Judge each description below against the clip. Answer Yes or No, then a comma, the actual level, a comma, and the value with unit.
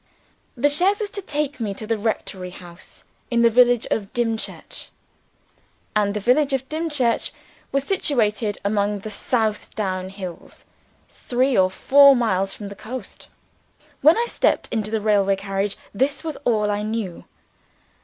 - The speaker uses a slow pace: No, average, 155 wpm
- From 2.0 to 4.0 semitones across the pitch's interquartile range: No, average, 4.8 semitones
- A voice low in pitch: No, high, 220 Hz